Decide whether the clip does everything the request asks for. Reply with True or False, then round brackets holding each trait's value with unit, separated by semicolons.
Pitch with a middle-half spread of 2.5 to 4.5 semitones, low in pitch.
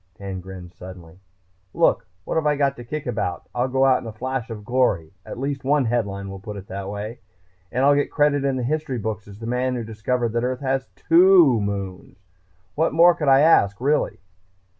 False (5.4 semitones; 125 Hz)